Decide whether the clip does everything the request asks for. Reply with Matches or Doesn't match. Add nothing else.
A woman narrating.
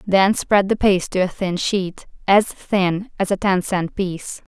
Matches